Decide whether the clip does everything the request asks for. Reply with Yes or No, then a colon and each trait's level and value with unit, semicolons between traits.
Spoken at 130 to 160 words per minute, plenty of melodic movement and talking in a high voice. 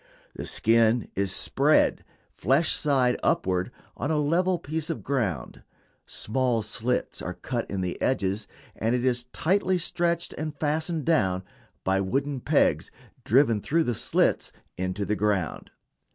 No: average, 140 wpm; wide, 7.1 semitones; low, 125 Hz